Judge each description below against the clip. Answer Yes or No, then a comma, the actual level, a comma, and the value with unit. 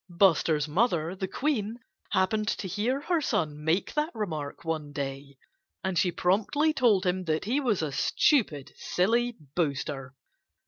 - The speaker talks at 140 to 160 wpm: Yes, average, 145 wpm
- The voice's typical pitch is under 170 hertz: No, medium, 185 Hz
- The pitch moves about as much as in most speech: No, wide, 6.7 semitones